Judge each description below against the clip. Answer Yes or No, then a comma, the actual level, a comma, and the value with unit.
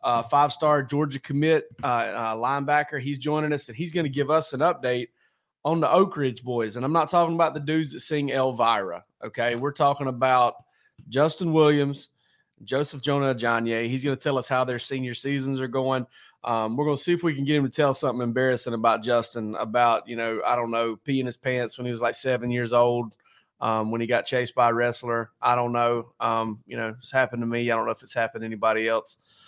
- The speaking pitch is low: Yes, low, 125 Hz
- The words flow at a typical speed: No, fast, 230 wpm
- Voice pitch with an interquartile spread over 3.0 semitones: Yes, average, 3.4 semitones